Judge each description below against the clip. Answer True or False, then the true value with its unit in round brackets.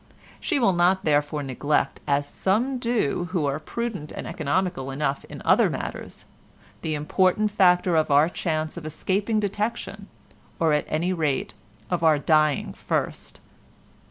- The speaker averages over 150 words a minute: False (135 wpm)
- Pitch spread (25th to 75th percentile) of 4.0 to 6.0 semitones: True (4.4 semitones)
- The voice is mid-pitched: True (165 Hz)